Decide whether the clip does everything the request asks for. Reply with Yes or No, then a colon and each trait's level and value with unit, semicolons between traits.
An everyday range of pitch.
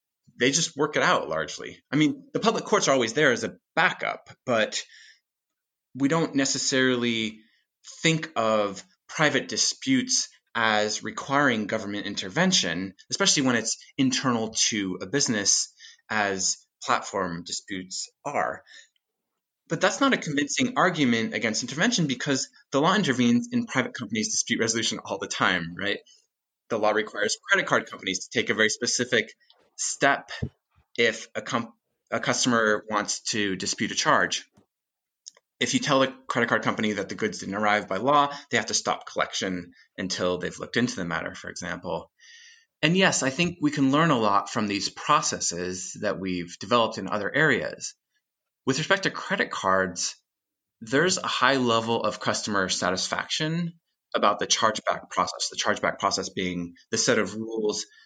No: wide, 7.8 semitones